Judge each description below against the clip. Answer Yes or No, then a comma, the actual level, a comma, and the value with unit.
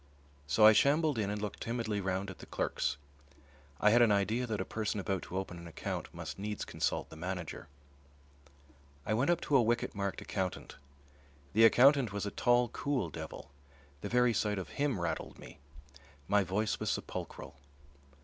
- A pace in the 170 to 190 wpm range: Yes, average, 180 wpm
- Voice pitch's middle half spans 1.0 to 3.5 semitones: No, average, 4.0 semitones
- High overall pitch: No, low, 105 Hz